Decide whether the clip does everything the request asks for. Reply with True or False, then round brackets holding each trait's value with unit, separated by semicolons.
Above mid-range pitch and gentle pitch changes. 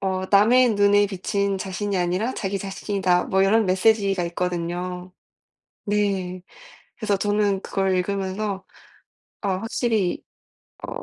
True (195 Hz; 1.8 semitones)